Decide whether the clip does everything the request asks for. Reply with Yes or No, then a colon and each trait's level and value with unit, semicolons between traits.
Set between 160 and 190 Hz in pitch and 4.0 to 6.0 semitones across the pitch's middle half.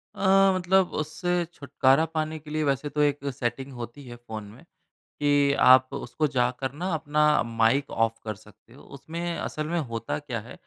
No: medium, 145 Hz; average, 4.4 semitones